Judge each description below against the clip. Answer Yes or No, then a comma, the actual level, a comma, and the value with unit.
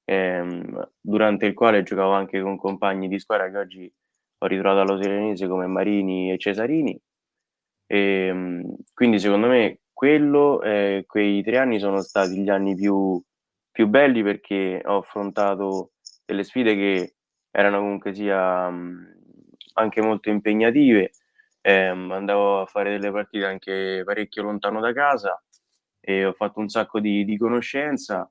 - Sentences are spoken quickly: No, average, 135 wpm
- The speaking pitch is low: Yes, low, 100 Hz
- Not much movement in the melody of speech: Yes, narrow, 1.7 semitones